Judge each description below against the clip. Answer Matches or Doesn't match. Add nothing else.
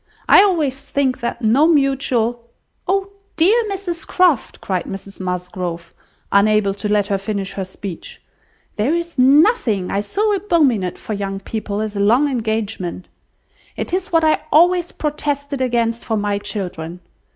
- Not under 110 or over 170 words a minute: Matches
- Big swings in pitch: Matches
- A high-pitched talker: Matches